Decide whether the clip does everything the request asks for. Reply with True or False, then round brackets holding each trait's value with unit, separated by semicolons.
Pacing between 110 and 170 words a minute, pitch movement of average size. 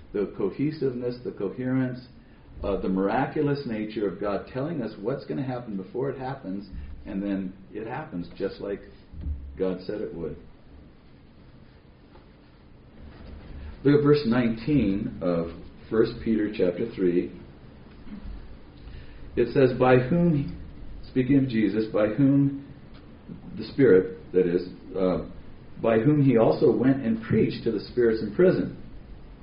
False (135 wpm; 8.2 semitones)